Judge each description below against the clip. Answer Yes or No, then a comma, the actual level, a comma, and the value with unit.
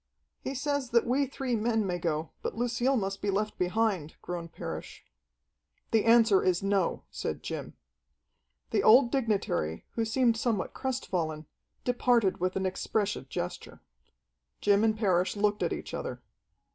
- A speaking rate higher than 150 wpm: No, average, 145 wpm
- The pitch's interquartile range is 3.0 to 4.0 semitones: No, average, 4.4 semitones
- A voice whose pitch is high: Yes, high, 210 Hz